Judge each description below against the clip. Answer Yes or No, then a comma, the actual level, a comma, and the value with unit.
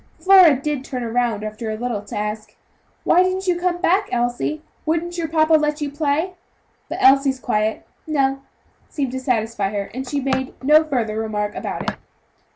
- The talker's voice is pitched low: No, very high, 270 Hz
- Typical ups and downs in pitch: No, wide, 5.7 semitones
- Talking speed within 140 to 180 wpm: Yes, average, 175 wpm